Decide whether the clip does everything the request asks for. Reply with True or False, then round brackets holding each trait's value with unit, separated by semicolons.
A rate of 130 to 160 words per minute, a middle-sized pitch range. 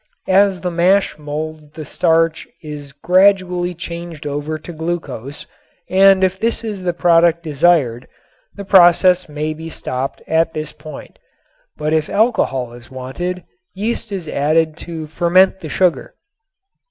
True (140 wpm; 3.2 semitones)